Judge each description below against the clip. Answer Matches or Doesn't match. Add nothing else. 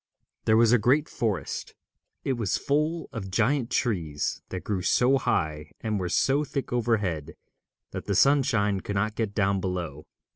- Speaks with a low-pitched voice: Matches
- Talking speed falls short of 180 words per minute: Matches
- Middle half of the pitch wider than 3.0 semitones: Matches